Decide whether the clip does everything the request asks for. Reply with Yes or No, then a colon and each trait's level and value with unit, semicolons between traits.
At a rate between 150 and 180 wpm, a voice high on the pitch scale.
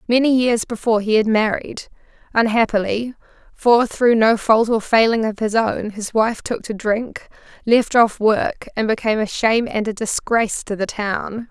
Yes: average, 175 wpm; high, 225 Hz